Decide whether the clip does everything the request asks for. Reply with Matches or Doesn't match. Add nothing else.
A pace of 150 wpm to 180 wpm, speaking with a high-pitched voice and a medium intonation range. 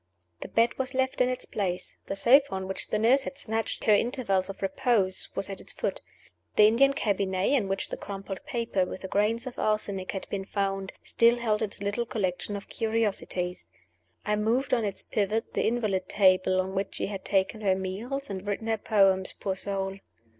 Doesn't match